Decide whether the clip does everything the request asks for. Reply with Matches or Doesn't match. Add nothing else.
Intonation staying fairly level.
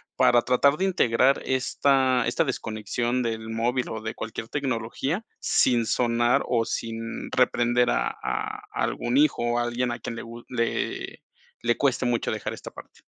Matches